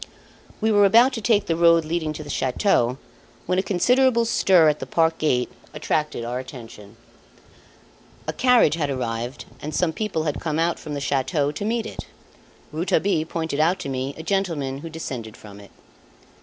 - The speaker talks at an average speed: Yes, average, 175 wpm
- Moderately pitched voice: Yes, medium, 155 Hz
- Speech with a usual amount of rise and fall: No, wide, 5.9 semitones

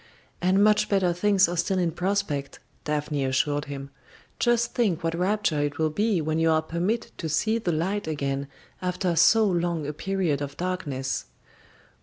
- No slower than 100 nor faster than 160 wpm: No, average, 170 wpm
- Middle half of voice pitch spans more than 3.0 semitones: Yes, average, 4.6 semitones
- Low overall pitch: No, medium, 170 Hz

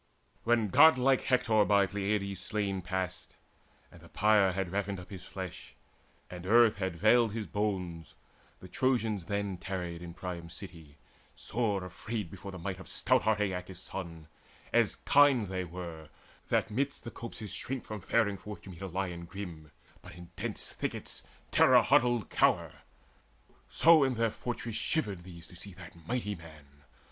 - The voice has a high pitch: No, low, 100 Hz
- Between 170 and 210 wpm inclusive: No, average, 160 wpm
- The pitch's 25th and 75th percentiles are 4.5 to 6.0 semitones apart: No, average, 3.6 semitones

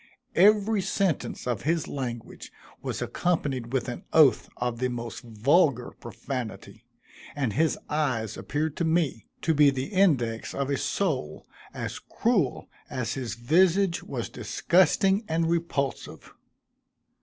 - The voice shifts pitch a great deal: Yes, wide, 5.8 semitones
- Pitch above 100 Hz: Yes, medium, 140 Hz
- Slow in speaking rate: Yes, slow, 130 wpm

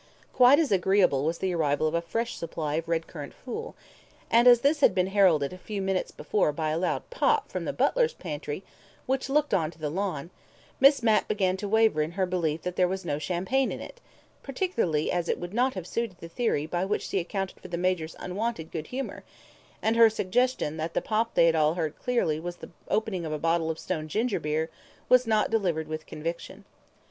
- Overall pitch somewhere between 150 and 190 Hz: Yes, medium, 185 Hz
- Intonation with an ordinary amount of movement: No, wide, 5.9 semitones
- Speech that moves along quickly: Yes, fast, 220 wpm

